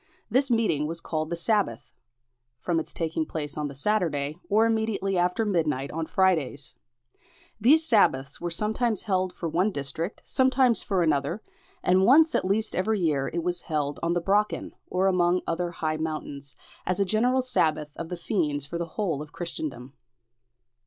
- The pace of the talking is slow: No, average, 170 wpm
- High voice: No, medium, 175 Hz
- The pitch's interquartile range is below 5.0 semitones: No, average, 5.3 semitones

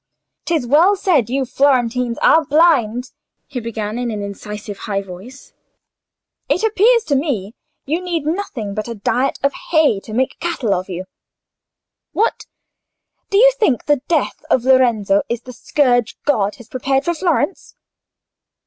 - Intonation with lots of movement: Yes, wide, 6.3 semitones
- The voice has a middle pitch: No, very high, 255 Hz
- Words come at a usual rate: Yes, average, 150 wpm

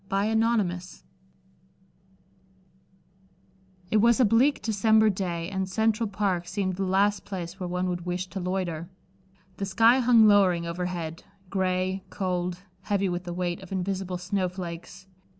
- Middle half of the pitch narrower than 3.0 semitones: Yes, narrow, 2.4 semitones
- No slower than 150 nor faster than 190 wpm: No, slow, 135 wpm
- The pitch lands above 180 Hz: Yes, high, 190 Hz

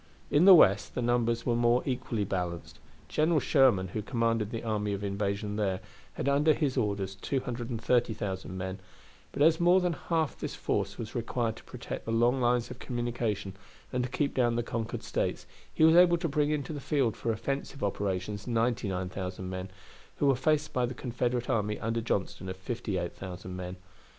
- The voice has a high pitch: No, low, 115 Hz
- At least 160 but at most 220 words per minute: Yes, average, 180 wpm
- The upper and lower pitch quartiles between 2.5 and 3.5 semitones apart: No, average, 4.6 semitones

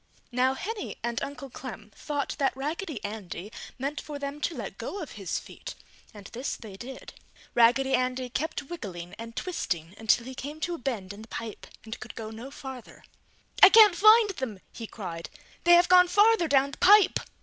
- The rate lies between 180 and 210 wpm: Yes, average, 190 wpm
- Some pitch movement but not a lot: No, wide, 6.3 semitones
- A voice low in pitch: No, very high, 265 Hz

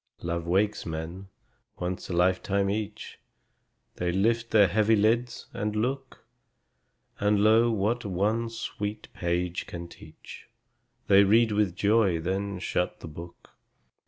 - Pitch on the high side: No, low, 100 Hz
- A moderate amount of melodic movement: Yes, average, 3.4 semitones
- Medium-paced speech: No, slow, 130 wpm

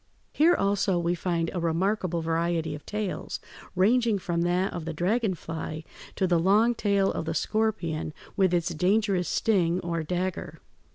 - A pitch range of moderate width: Yes, average, 3.2 semitones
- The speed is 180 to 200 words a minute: No, average, 160 wpm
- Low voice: No, medium, 180 Hz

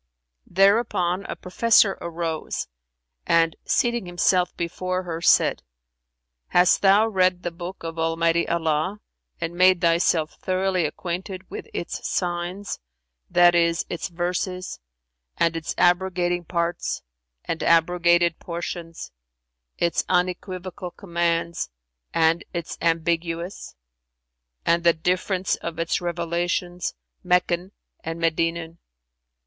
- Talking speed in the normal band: No, slow, 105 wpm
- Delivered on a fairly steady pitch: Yes, narrow, 1.5 semitones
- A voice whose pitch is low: No, medium, 175 Hz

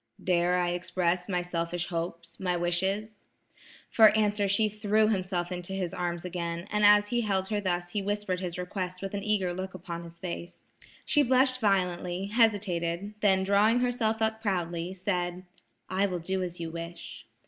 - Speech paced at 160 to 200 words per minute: Yes, average, 170 wpm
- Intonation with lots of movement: No, average, 2.8 semitones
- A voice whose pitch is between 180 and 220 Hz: Yes, medium, 185 Hz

